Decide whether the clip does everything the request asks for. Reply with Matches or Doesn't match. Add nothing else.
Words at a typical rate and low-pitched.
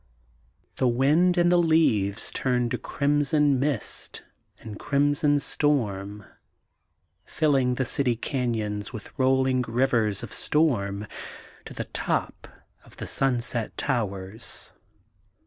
Doesn't match